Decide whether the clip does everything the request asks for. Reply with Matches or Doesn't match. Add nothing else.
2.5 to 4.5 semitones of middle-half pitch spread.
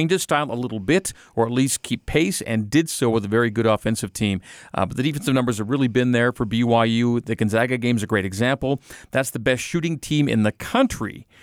Matches